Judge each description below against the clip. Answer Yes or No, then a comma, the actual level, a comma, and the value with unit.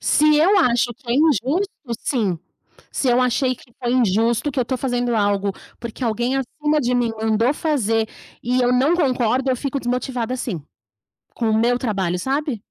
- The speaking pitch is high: Yes, high, 245 Hz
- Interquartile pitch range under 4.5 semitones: Yes, average, 2.9 semitones